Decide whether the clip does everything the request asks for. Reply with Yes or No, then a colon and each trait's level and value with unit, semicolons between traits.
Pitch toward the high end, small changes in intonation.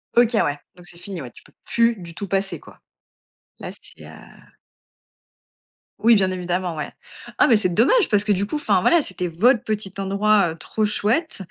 No: high, 200 Hz; average, 3.4 semitones